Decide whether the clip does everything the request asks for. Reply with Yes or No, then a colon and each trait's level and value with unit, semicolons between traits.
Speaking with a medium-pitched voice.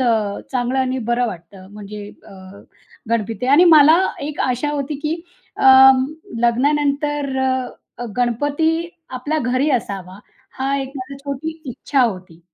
No: very high, 260 Hz